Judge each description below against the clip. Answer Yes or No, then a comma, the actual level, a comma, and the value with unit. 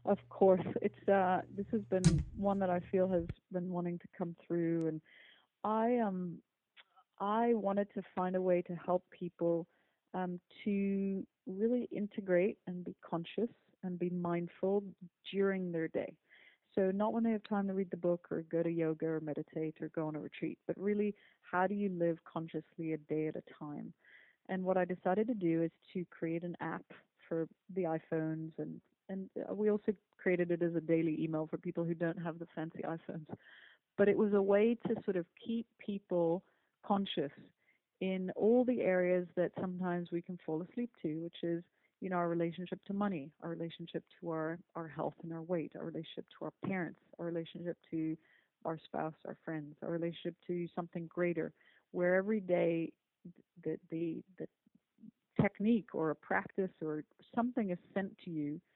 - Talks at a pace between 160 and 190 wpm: Yes, average, 185 wpm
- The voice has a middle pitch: Yes, medium, 180 Hz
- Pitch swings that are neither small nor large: Yes, average, 3.0 semitones